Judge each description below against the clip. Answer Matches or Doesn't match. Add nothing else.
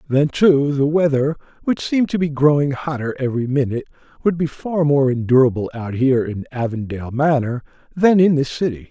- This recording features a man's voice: Matches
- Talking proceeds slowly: Doesn't match